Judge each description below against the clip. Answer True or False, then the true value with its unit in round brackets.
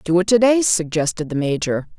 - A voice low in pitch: False (180 Hz)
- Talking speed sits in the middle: False (210 wpm)